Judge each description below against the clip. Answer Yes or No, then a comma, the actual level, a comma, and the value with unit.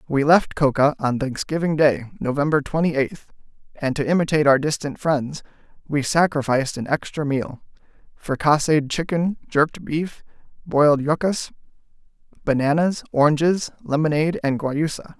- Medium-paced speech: No, slow, 120 wpm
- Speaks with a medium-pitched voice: Yes, medium, 150 Hz